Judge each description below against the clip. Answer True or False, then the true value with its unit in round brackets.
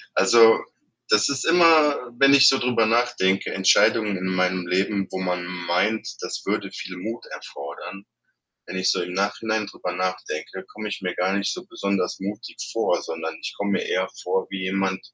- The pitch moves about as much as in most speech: True (3.2 semitones)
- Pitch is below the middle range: True (95 Hz)